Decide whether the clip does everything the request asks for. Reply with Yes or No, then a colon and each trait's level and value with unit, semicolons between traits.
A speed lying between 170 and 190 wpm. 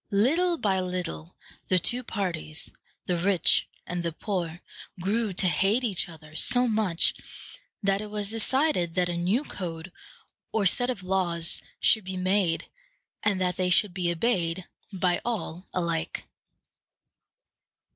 No: average, 140 wpm